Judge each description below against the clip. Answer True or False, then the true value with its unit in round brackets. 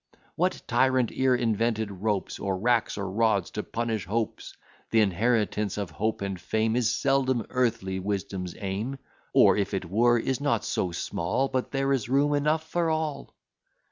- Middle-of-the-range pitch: False (115 Hz)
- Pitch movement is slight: False (4.7 semitones)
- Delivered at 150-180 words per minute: True (165 wpm)